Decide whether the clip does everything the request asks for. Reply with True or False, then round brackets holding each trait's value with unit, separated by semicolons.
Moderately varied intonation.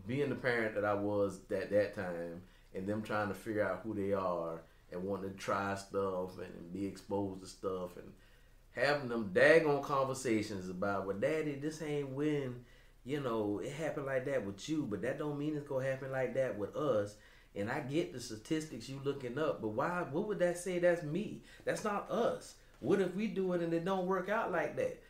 False (7.4 semitones)